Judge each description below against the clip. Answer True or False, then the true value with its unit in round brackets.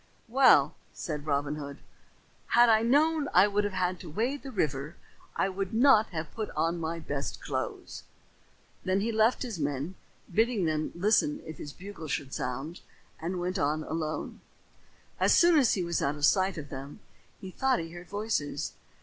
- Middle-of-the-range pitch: True (180 Hz)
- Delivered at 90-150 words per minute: False (175 wpm)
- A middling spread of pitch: False (6.3 semitones)